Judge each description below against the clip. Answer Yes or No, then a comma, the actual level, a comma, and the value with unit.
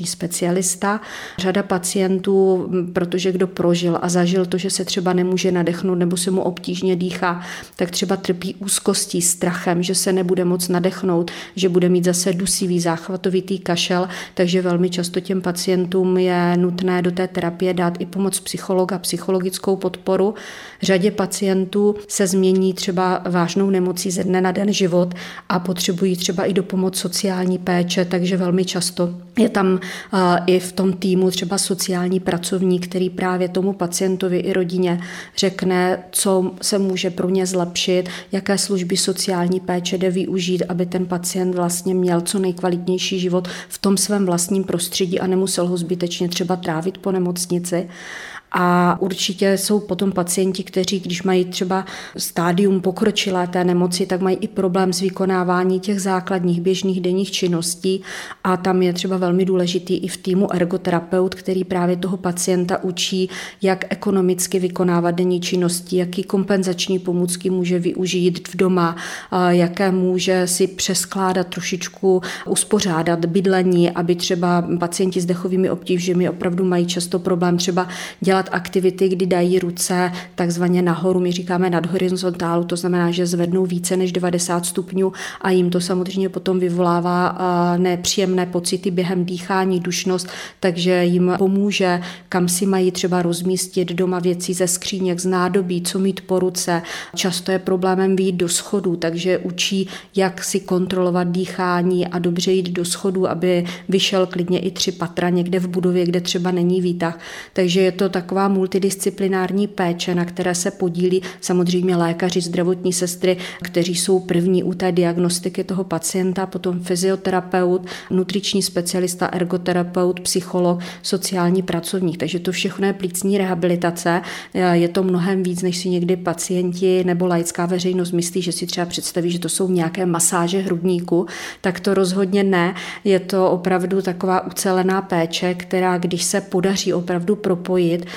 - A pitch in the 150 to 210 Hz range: Yes, medium, 185 Hz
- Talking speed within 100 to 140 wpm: No, average, 150 wpm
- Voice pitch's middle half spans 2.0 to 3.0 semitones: No, narrow, 1.1 semitones